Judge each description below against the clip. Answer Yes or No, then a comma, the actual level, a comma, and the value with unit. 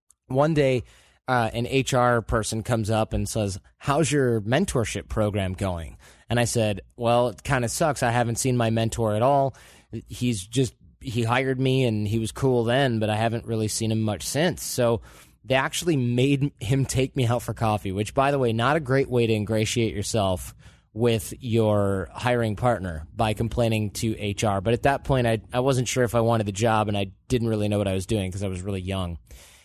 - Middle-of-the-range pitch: No, low, 115 Hz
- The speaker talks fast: Yes, fast, 210 wpm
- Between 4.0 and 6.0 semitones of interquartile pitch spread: No, average, 2.9 semitones